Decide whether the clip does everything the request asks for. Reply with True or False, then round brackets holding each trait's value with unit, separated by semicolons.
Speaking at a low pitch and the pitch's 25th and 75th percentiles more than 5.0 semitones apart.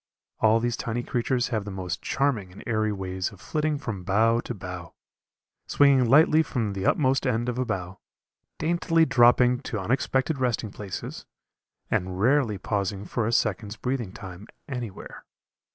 False (115 Hz; 4.7 semitones)